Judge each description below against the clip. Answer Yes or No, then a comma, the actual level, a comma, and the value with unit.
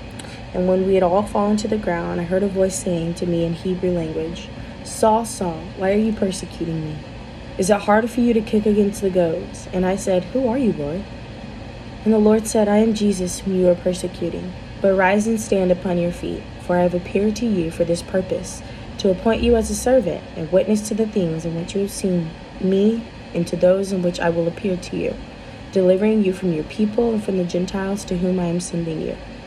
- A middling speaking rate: No, fast, 230 wpm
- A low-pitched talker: No, medium, 185 Hz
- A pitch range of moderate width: Yes, average, 3.5 semitones